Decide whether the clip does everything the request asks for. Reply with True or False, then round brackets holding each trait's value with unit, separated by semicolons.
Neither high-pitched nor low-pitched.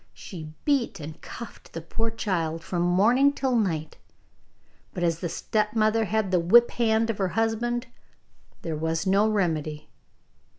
False (200 Hz)